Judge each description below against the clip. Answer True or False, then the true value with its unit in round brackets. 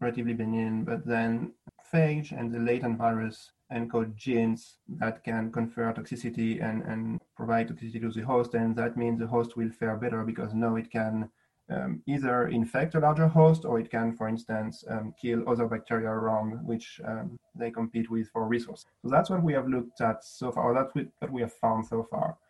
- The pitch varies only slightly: True (1.2 semitones)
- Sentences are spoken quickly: False (195 wpm)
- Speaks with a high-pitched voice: False (115 Hz)